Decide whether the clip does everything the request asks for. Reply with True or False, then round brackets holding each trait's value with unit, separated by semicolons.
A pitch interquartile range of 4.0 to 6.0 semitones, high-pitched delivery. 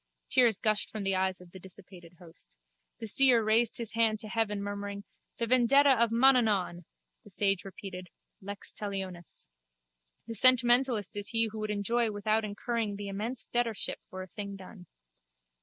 False (2.9 semitones; 210 Hz)